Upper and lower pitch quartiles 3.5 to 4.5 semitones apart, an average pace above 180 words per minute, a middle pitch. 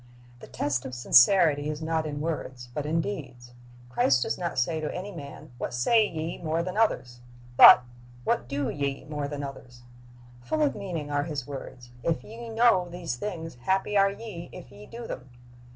No: wide, 5.5 semitones; average, 190 wpm; medium, 155 Hz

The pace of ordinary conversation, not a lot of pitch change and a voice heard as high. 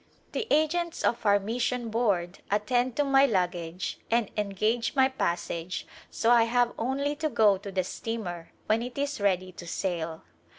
No: average, 170 wpm; average, 5.1 semitones; high, 225 Hz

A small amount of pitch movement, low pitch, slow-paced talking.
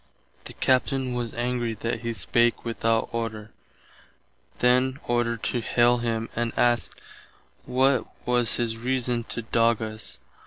Yes: narrow, 1.4 semitones; low, 120 Hz; slow, 130 wpm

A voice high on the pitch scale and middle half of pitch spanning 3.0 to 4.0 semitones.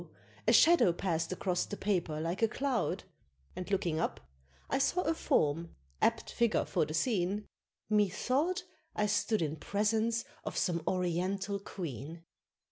No: high, 195 Hz; average, 4.7 semitones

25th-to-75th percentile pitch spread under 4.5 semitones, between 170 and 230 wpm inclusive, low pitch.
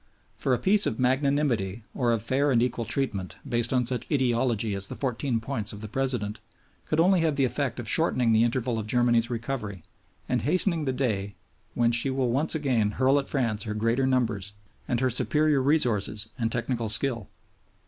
Yes: average, 3.3 semitones; average, 190 wpm; low, 120 Hz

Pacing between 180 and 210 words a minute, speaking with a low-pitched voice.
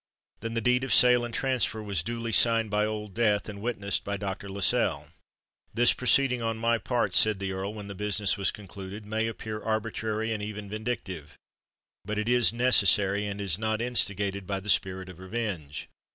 Yes: average, 185 wpm; low, 105 Hz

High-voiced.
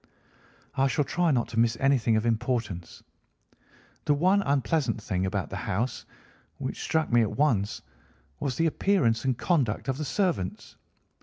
No: low, 125 Hz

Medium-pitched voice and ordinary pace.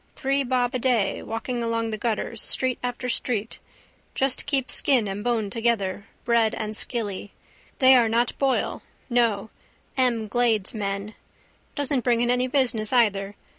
No: high, 235 Hz; average, 145 wpm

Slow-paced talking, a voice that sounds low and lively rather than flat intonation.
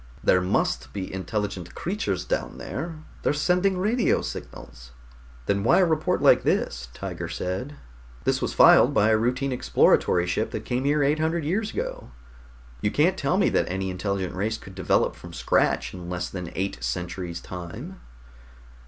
No: average, 165 wpm; low, 105 Hz; wide, 8.8 semitones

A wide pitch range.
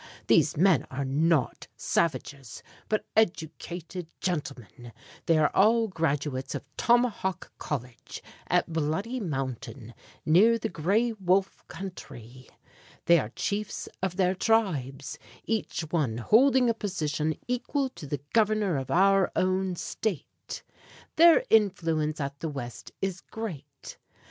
Yes: wide, 6.6 semitones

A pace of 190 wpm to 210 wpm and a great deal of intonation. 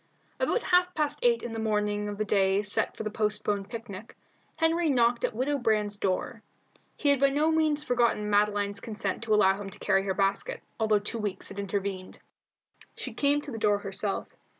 No: average, 195 wpm; average, 4.1 semitones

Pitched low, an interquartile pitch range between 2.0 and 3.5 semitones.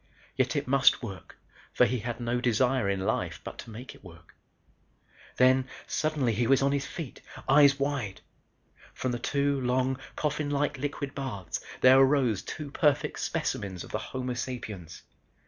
Yes: low, 130 Hz; average, 2.9 semitones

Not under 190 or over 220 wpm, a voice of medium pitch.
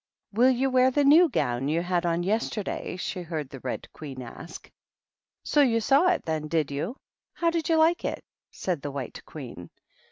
Yes: average, 200 wpm; medium, 180 Hz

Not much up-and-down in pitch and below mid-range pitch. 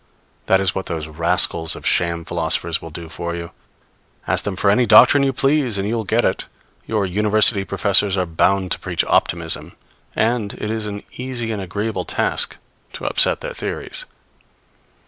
No: average, 4.5 semitones; low, 100 Hz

